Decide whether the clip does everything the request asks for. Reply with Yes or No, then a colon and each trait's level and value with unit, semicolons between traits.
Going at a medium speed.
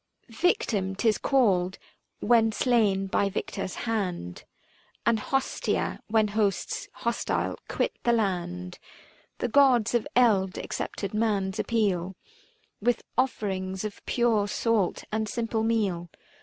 No: slow, 115 wpm